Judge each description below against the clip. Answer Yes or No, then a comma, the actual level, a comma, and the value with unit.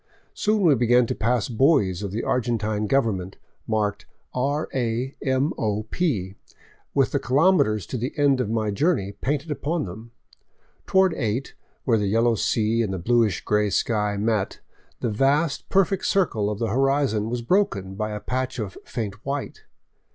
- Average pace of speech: Yes, average, 170 wpm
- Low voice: Yes, low, 115 Hz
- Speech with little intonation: No, average, 4.6 semitones